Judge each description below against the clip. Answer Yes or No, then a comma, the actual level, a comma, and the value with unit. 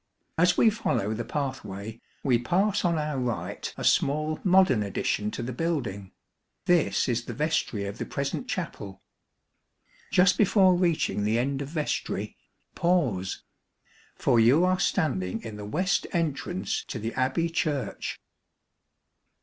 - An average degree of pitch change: No, wide, 7.6 semitones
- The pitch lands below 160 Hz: Yes, medium, 140 Hz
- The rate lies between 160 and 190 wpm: No, average, 140 wpm